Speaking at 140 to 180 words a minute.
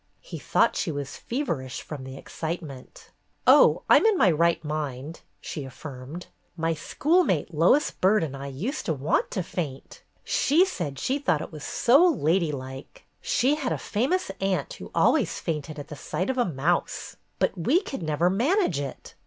Yes: average, 170 wpm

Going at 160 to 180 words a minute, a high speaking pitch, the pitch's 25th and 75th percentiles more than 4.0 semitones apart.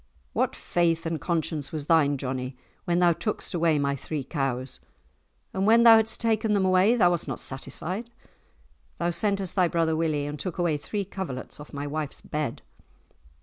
No: average, 175 wpm; medium, 165 Hz; average, 4.6 semitones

